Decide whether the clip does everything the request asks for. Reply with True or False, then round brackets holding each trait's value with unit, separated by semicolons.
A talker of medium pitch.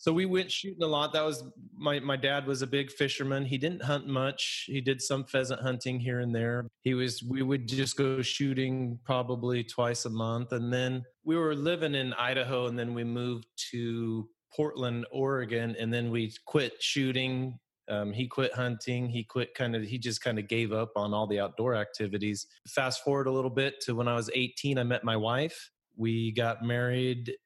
False (125 Hz)